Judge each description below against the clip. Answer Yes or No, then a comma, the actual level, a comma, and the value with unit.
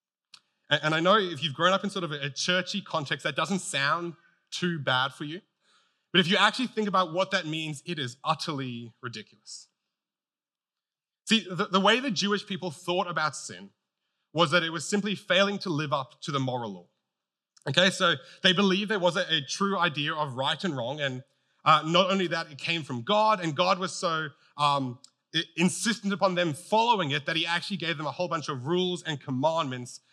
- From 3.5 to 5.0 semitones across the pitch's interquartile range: Yes, average, 4.3 semitones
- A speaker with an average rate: Yes, average, 195 wpm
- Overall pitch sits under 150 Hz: No, medium, 170 Hz